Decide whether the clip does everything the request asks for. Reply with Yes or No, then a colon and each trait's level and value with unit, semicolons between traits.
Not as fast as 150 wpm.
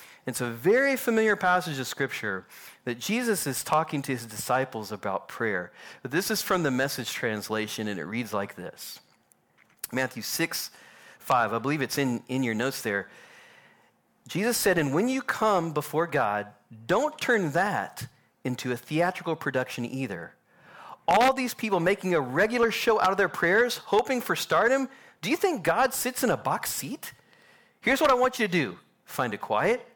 No: average, 175 wpm